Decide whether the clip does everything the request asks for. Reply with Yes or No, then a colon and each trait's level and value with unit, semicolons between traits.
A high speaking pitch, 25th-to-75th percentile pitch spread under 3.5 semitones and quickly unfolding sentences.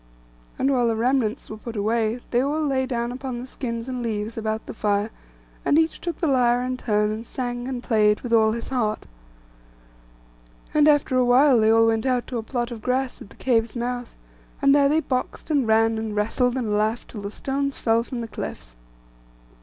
Yes: high, 240 Hz; average, 2.8 semitones; fast, 210 wpm